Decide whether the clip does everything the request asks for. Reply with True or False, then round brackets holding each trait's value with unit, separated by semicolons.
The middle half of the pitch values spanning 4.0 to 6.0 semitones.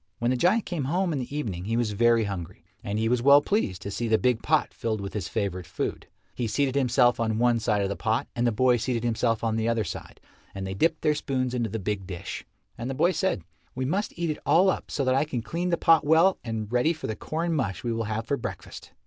True (4.7 semitones)